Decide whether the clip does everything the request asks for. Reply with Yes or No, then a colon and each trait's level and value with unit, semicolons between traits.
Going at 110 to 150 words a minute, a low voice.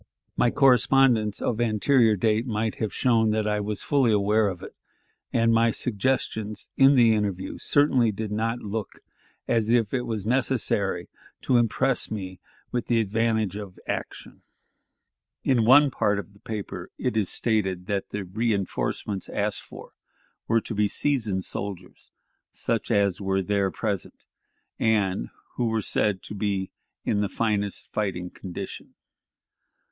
Yes: average, 145 wpm; low, 110 Hz